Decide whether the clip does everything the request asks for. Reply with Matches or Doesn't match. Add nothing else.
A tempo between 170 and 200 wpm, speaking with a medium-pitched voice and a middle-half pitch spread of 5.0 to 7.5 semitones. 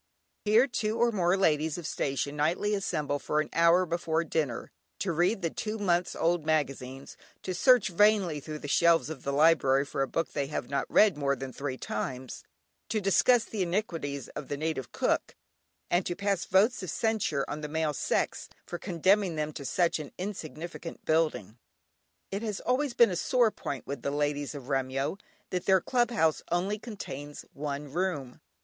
Matches